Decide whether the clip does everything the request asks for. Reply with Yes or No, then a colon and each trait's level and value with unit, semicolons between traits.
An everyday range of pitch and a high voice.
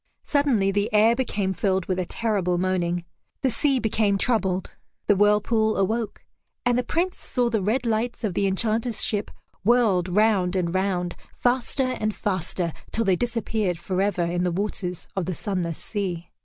Yes: average, 3.7 semitones; high, 205 Hz